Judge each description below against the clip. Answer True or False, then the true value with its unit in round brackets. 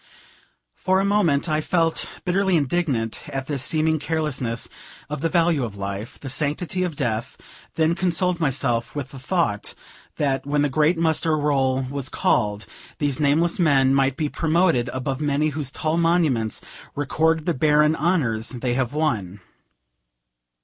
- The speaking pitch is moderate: True (145 Hz)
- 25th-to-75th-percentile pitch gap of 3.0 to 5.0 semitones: True (3.8 semitones)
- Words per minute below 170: True (150 wpm)